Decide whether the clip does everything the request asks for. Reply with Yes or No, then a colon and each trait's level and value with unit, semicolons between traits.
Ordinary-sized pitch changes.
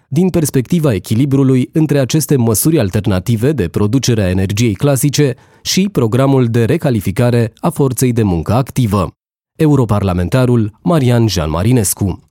Yes: average, 4.7 semitones